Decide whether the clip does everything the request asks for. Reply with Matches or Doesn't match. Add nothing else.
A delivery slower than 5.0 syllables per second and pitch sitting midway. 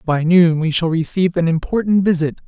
Doesn't match